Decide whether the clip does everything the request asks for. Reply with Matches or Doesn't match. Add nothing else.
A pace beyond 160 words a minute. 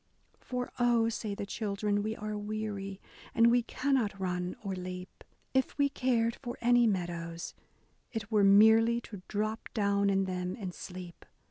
Doesn't match